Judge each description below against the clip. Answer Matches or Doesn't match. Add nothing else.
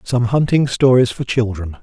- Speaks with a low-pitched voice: Matches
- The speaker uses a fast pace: Doesn't match